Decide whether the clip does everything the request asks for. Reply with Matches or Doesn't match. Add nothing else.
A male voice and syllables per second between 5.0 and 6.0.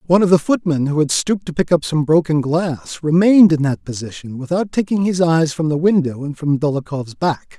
Matches